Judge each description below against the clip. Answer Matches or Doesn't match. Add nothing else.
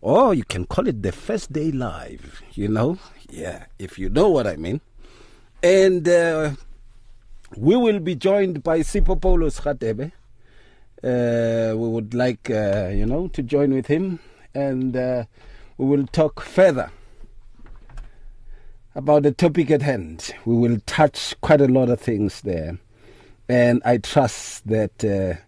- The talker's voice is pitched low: Matches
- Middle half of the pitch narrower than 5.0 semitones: Doesn't match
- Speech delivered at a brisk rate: Doesn't match